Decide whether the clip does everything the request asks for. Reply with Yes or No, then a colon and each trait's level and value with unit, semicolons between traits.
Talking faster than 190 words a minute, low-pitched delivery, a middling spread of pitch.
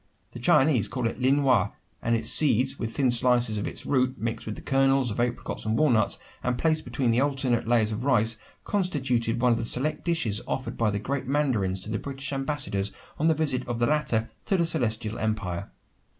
Yes: average, 200 wpm; low, 125 Hz; average, 3.6 semitones